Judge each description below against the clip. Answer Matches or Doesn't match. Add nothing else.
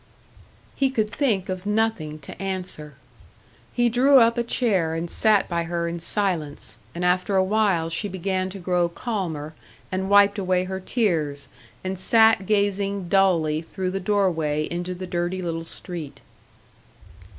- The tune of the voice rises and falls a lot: Doesn't match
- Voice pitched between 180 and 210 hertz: Matches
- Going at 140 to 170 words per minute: Matches